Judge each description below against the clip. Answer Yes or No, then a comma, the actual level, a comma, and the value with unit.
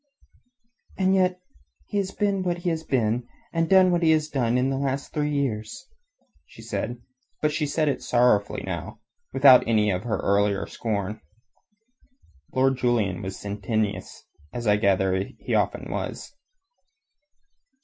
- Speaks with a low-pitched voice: Yes, low, 125 Hz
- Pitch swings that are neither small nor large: No, wide, 6.7 semitones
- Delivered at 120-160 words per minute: Yes, average, 150 wpm